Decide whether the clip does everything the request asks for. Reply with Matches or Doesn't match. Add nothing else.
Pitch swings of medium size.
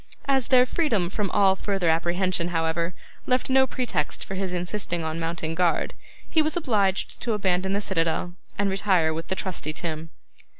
Matches